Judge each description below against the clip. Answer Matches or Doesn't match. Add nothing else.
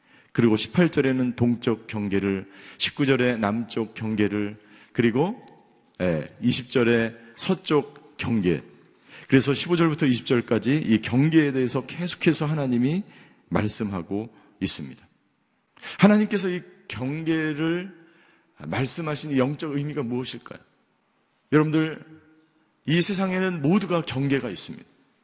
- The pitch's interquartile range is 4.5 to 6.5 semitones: Matches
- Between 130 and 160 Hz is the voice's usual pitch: Matches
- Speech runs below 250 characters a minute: Matches